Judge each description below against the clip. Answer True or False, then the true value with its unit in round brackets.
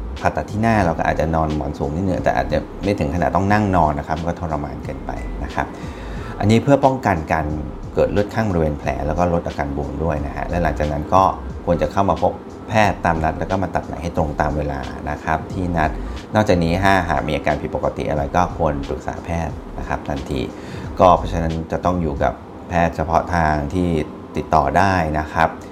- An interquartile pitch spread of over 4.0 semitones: False (3.0 semitones)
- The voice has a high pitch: False (80 Hz)